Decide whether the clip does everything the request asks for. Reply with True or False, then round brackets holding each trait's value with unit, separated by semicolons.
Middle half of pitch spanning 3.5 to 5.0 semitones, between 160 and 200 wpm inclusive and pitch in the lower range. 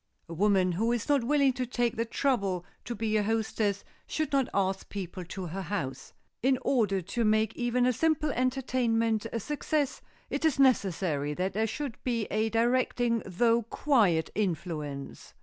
False (4.6 semitones; 165 wpm; 225 Hz)